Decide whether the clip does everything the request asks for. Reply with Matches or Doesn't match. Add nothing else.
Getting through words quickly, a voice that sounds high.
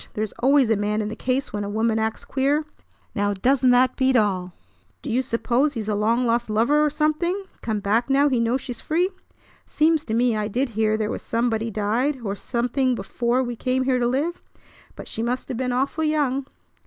Matches